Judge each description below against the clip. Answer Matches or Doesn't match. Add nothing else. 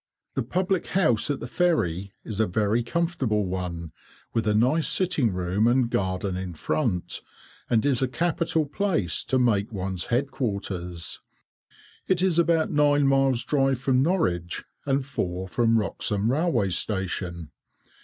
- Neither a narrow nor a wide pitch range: Doesn't match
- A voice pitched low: Matches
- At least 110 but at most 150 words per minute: Matches